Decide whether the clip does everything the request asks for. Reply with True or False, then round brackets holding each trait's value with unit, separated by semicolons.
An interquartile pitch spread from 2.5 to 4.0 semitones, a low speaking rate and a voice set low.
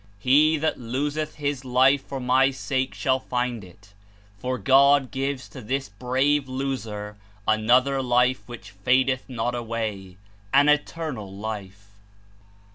True (3.7 semitones; 125 wpm; 130 Hz)